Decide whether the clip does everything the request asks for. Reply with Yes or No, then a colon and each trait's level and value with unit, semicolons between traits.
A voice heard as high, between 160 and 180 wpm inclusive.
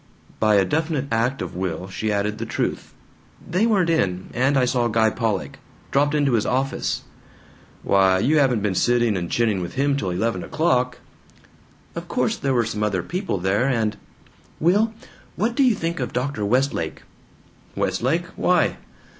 No: low, 120 Hz; average, 165 wpm